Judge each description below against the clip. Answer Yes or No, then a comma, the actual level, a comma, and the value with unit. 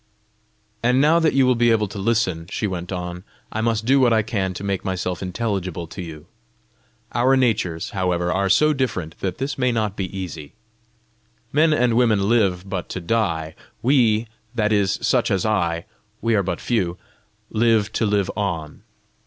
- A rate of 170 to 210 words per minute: Yes, average, 180 wpm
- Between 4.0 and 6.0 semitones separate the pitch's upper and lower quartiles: Yes, average, 4.5 semitones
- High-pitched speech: No, low, 100 Hz